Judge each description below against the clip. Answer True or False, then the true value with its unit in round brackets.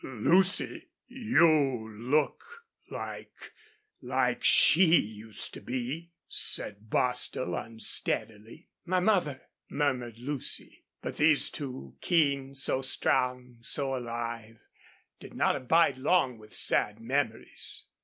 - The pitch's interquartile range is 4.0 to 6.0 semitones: True (5.0 semitones)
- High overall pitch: False (130 Hz)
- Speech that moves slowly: True (105 wpm)